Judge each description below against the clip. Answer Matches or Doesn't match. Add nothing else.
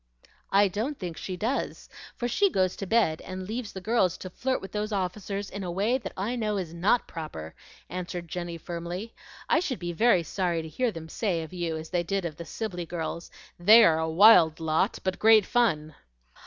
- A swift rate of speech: Matches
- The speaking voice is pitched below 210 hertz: Matches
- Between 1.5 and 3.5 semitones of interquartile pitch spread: Doesn't match